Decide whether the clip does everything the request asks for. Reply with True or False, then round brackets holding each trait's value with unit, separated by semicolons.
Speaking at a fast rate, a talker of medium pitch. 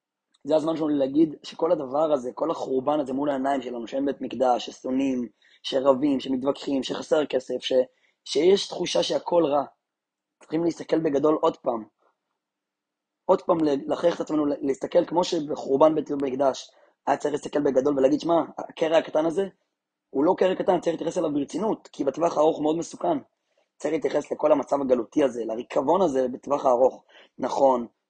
True (160 wpm; 145 Hz)